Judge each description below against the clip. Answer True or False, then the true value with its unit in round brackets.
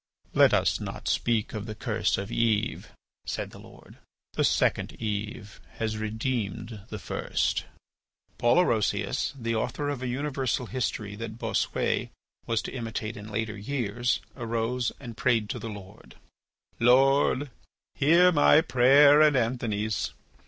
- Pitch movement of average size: True (3.2 semitones)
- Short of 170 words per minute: True (140 wpm)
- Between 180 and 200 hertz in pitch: False (115 Hz)